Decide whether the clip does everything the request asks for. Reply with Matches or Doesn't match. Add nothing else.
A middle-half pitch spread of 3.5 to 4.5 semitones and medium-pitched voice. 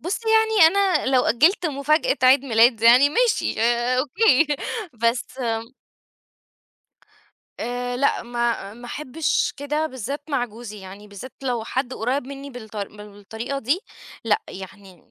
Doesn't match